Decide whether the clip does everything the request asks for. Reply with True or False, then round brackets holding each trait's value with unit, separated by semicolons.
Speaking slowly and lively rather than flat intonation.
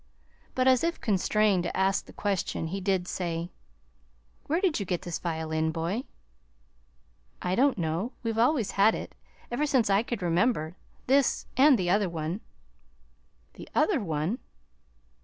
False (150 wpm; 5.9 semitones)